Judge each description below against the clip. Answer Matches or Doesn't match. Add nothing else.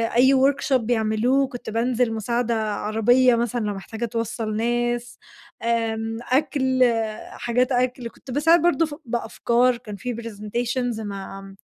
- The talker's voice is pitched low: Doesn't match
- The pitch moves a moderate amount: Doesn't match